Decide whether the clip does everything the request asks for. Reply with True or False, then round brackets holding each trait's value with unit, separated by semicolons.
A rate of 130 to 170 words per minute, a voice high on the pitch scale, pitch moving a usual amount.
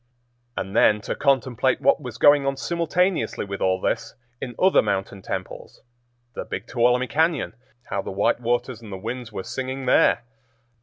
False (160 wpm; 125 Hz; 4.2 semitones)